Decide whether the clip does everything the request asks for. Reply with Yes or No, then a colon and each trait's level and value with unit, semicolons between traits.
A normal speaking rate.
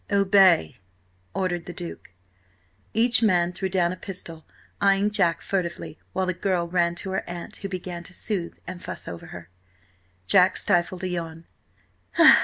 Yes: average, 155 wpm